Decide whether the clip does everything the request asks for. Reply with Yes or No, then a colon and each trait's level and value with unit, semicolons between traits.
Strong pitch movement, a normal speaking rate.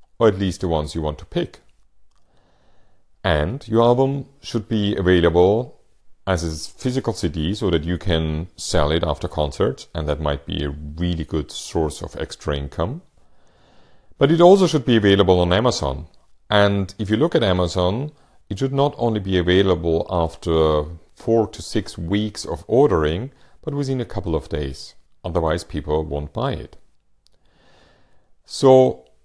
Yes: wide, 5.8 semitones; average, 160 wpm